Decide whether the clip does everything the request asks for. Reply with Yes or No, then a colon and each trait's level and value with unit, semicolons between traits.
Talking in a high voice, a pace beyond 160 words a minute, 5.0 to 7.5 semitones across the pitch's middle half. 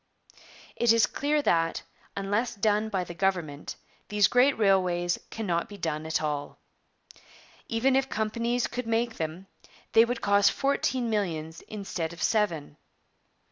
No: high, 205 Hz; average, 140 wpm; average, 5.3 semitones